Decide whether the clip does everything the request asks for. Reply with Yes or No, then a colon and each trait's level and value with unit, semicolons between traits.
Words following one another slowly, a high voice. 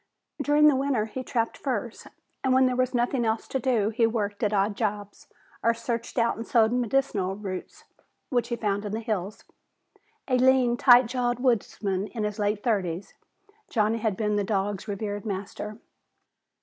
No: average, 175 wpm; high, 225 Hz